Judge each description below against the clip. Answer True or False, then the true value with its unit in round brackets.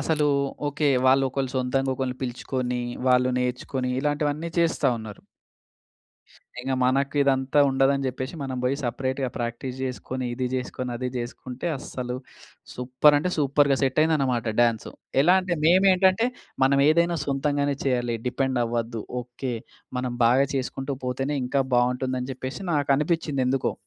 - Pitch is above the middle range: False (130 Hz)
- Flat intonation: True (2.3 semitones)